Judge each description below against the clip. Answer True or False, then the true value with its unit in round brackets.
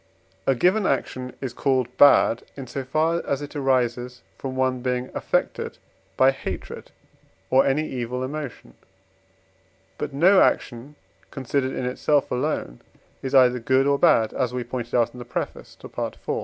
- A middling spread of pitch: False (2.1 semitones)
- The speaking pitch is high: False (130 Hz)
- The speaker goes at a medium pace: True (160 wpm)